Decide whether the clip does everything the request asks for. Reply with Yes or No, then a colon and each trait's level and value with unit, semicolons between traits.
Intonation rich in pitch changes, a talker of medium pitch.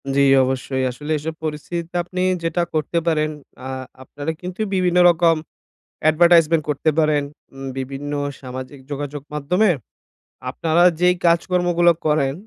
No: average, 3.3 semitones; medium, 155 Hz